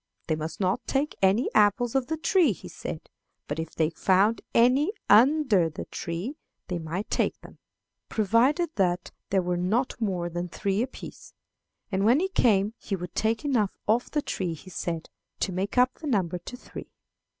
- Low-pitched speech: No, high, 205 Hz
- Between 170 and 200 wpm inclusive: Yes, average, 180 wpm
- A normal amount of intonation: No, wide, 5.9 semitones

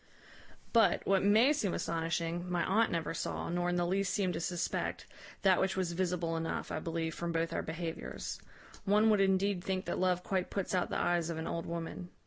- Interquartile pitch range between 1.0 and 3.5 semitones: Yes, narrow, 2.5 semitones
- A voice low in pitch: No, medium, 175 Hz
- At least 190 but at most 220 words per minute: Yes, fast, 205 wpm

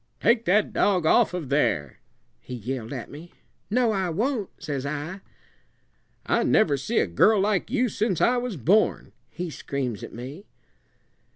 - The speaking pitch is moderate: Yes, medium, 175 Hz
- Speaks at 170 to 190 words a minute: No, average, 160 wpm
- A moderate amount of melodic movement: No, wide, 7.6 semitones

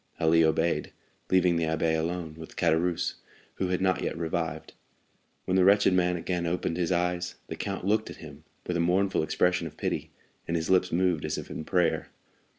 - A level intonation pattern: Yes, narrow, 1.9 semitones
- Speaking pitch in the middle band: No, very low, 85 Hz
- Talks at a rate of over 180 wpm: Yes, average, 190 wpm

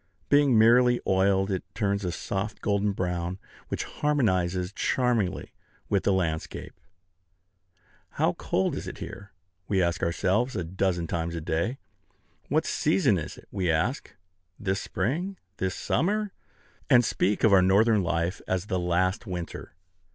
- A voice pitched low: Yes, very low, 95 Hz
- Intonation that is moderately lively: Yes, average, 3.8 semitones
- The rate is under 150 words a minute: Yes, average, 140 wpm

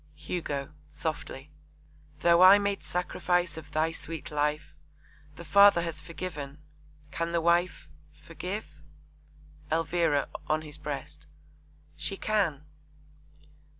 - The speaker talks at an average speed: No, slow, 105 wpm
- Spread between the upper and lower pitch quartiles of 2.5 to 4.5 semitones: Yes, average, 2.9 semitones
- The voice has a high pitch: No, medium, 165 Hz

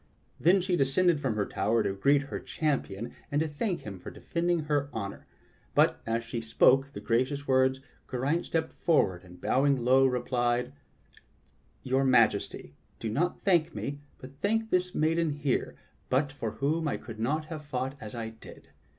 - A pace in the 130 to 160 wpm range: No, average, 170 wpm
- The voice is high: No, low, 135 Hz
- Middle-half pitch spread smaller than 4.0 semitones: No, average, 4.9 semitones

